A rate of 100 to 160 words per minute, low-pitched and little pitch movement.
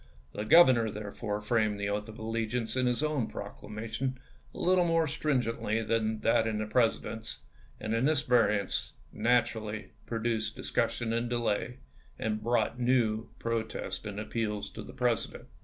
Yes: average, 155 wpm; low, 115 Hz; narrow, 2.2 semitones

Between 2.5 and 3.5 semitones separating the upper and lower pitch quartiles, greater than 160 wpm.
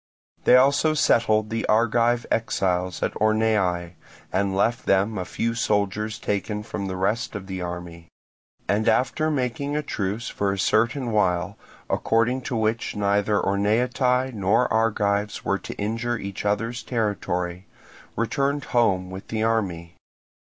No: average, 3.1 semitones; average, 140 wpm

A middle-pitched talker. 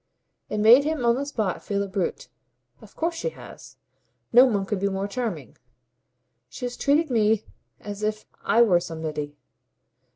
No: high, 215 Hz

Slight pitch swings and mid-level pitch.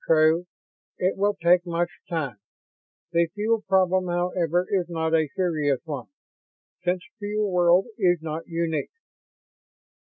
Yes: narrow, 2.3 semitones; medium, 175 Hz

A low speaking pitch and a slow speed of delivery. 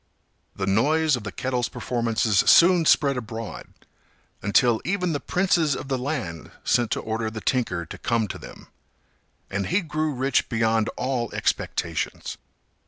No: low, 125 Hz; average, 150 wpm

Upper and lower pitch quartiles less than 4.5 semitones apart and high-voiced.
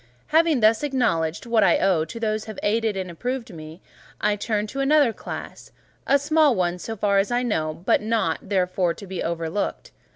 No: average, 5.1 semitones; high, 210 Hz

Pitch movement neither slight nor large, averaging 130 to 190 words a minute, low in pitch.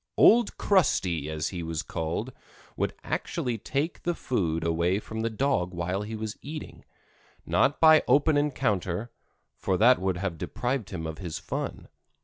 No: wide, 7.7 semitones; average, 155 wpm; low, 105 Hz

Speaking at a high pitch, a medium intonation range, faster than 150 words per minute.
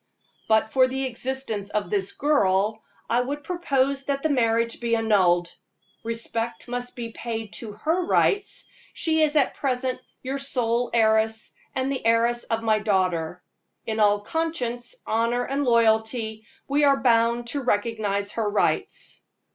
No: high, 230 Hz; average, 3.4 semitones; average, 145 wpm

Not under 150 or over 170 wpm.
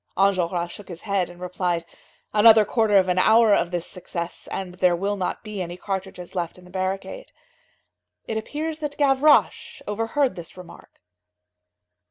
Yes: average, 160 wpm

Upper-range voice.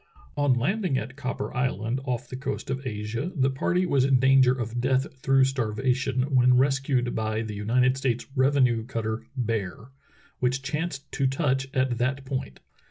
No: low, 130 Hz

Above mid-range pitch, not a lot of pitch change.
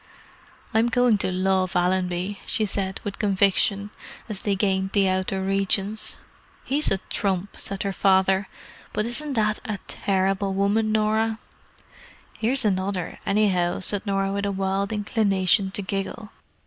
Yes: high, 200 Hz; narrow, 1.9 semitones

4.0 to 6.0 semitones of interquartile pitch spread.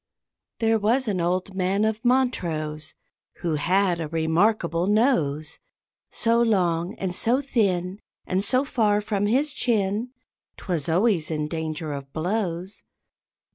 Yes: average, 5.2 semitones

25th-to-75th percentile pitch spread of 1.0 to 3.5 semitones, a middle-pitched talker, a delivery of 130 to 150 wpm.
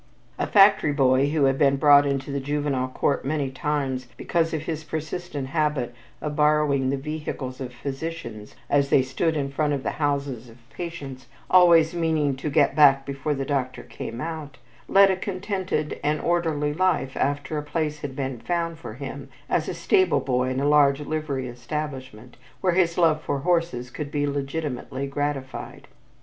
No: average, 2.7 semitones; medium, 145 Hz; average, 170 wpm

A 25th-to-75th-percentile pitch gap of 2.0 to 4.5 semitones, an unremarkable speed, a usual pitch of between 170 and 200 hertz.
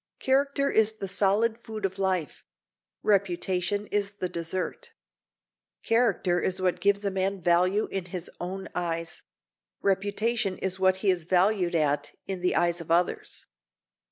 Yes: narrow, 2.4 semitones; average, 145 wpm; high, 190 Hz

